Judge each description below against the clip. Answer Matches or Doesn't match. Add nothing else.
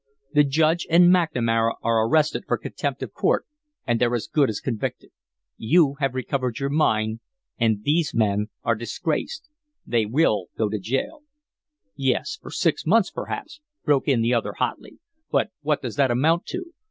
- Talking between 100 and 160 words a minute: Doesn't match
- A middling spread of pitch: Doesn't match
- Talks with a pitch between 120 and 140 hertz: Matches